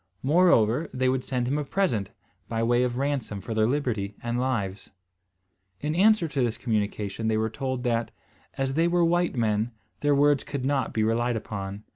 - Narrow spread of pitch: No, average, 4.5 semitones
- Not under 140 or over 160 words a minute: No, average, 185 wpm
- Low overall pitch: Yes, low, 125 Hz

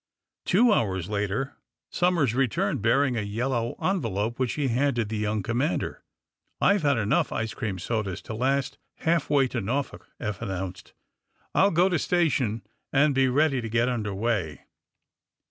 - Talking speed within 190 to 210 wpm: No, average, 155 wpm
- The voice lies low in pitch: Yes, low, 120 Hz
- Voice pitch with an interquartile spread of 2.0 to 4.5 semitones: No, average, 4.9 semitones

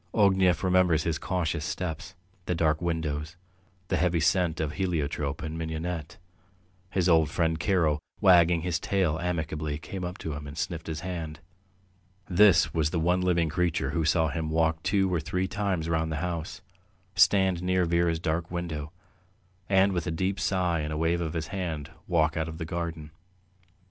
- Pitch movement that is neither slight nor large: No, narrow, 2.3 semitones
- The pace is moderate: Yes, average, 175 wpm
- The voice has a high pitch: No, very low, 85 Hz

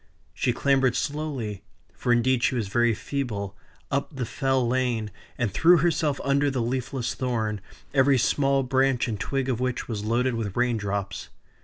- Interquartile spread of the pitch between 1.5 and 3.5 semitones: Yes, average, 3.1 semitones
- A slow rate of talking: No, average, 165 wpm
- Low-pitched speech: Yes, low, 125 Hz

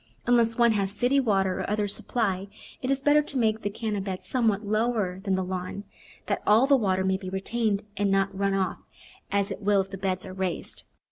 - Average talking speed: No, fast, 215 wpm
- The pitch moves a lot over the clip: No, average, 3.0 semitones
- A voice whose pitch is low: No, high, 200 Hz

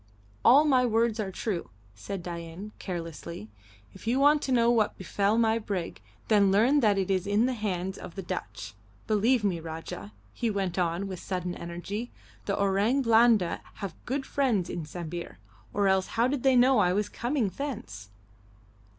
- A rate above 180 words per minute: No, average, 175 wpm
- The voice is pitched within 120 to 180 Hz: No, high, 200 Hz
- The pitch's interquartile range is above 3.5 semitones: Yes, average, 4.9 semitones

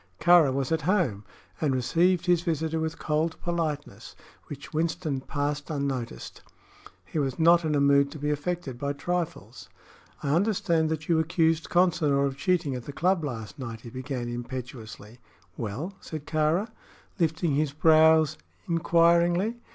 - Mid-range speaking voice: Yes, medium, 155 Hz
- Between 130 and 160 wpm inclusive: Yes, average, 150 wpm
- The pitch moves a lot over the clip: No, average, 3.4 semitones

